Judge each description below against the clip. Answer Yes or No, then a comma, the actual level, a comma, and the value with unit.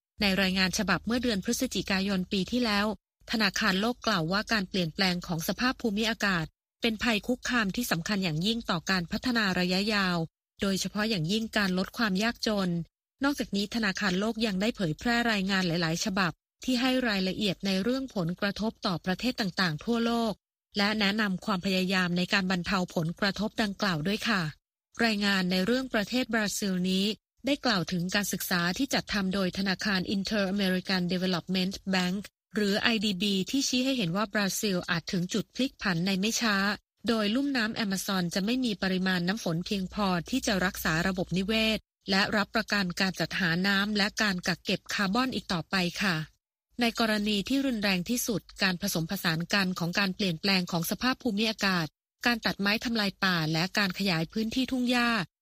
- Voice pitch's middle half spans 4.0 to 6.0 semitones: No, average, 3.2 semitones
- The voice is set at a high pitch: Yes, high, 200 Hz